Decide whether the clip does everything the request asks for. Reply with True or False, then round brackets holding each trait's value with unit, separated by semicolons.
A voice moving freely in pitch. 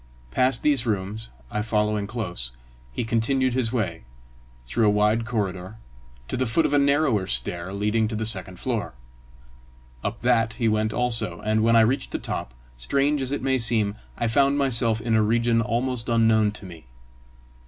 False (2.8 semitones)